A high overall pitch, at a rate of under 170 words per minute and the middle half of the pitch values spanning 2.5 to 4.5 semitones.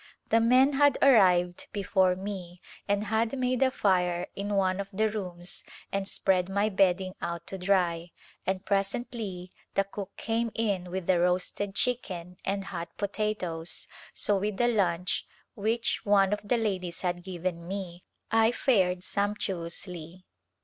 Yes: high, 195 Hz; average, 150 wpm; average, 2.8 semitones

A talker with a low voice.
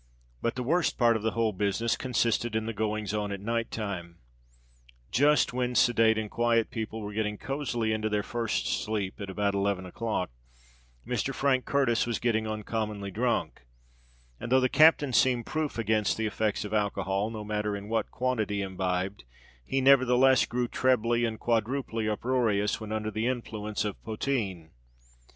Yes: low, 110 Hz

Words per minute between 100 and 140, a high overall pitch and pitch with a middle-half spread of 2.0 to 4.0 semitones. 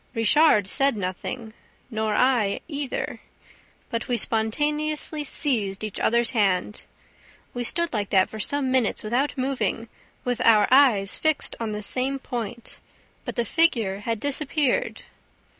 No: slow, 135 wpm; high, 235 Hz; average, 4.6 semitones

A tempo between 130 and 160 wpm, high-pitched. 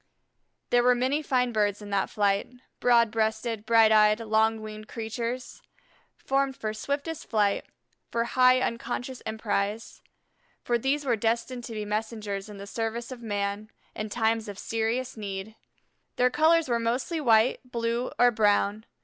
Yes: average, 150 wpm; high, 225 Hz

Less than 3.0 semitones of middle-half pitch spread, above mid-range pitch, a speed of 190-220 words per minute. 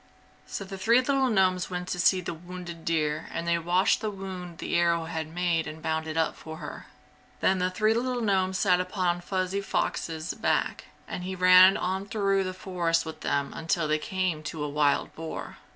No: narrow, 2.6 semitones; medium, 180 Hz; average, 200 wpm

